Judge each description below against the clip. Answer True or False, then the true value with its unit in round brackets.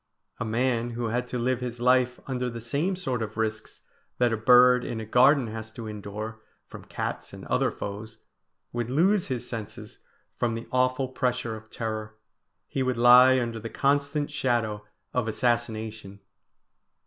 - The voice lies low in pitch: True (120 Hz)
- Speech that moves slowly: False (165 wpm)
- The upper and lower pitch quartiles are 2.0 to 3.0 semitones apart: True (2.4 semitones)